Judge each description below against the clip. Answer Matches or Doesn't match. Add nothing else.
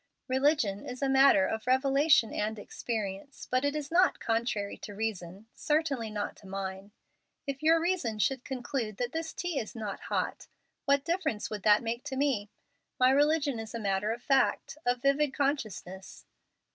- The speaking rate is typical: Matches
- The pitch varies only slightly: Doesn't match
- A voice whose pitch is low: Doesn't match